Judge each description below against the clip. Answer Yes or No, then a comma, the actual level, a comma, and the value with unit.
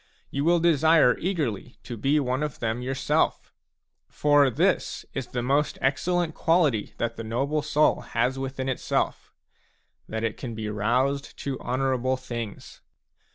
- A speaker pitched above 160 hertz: No, low, 130 Hz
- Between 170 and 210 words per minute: No, average, 145 wpm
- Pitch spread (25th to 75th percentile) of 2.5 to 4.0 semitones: Yes, average, 3.7 semitones